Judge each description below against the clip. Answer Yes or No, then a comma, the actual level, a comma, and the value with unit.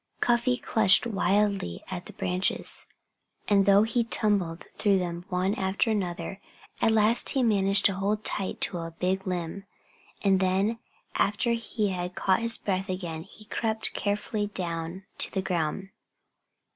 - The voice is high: Yes, high, 195 Hz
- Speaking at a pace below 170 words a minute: Yes, average, 150 wpm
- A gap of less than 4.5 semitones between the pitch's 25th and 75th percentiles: Yes, average, 2.7 semitones